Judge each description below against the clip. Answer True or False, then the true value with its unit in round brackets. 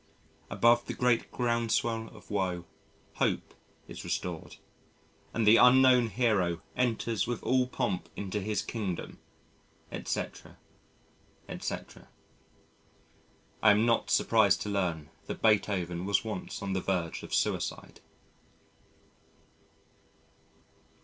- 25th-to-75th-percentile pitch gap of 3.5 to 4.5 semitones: True (3.8 semitones)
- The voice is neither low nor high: False (105 Hz)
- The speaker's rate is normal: False (105 wpm)